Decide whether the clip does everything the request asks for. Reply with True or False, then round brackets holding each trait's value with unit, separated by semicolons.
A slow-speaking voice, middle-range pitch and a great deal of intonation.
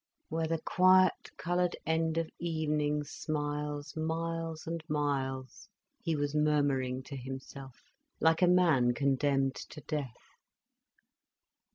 False (110 wpm; 150 Hz; 2.9 semitones)